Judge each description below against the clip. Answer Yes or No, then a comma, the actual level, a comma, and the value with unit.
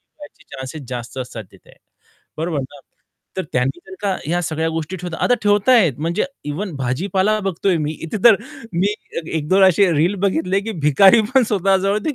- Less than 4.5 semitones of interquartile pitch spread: No, average, 4.8 semitones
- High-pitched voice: No, medium, 175 Hz